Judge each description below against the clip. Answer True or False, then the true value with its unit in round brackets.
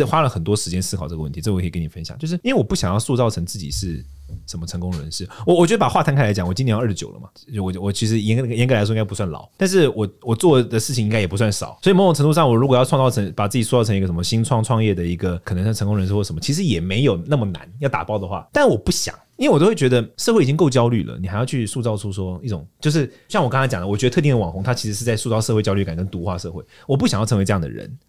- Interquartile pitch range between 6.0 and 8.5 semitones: False (5.2 semitones)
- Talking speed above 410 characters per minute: True (455 characters per minute)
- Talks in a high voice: False (110 Hz)